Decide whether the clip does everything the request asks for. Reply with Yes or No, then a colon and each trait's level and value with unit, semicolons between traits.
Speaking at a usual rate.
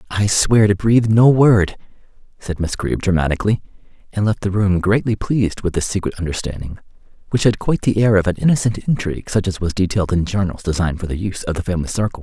No: fast, 210 wpm